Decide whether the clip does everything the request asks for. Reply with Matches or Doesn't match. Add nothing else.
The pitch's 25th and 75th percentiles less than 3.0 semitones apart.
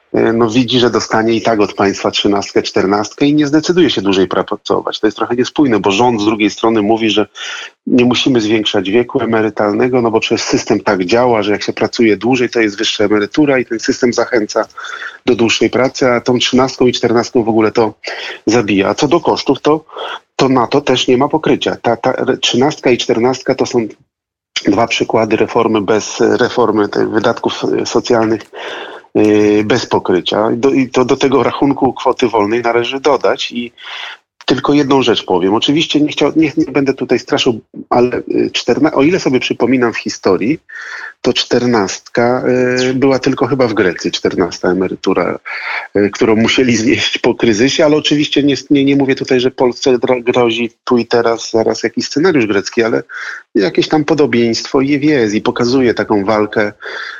Doesn't match